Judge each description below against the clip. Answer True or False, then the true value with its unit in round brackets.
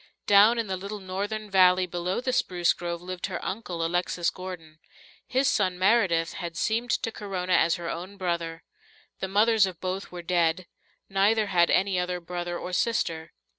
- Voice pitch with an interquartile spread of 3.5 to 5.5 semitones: False (2.6 semitones)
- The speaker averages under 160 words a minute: False (170 wpm)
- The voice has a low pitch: False (185 Hz)